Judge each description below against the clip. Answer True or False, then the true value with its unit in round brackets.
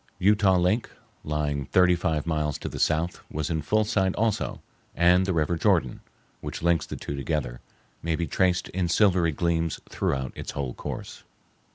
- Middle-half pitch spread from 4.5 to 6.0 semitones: False (3.3 semitones)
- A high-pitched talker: False (85 Hz)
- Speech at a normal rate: True (170 wpm)